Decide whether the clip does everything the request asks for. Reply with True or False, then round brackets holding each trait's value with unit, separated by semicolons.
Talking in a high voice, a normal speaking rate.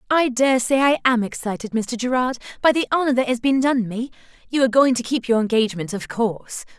False (245 Hz; 220 wpm)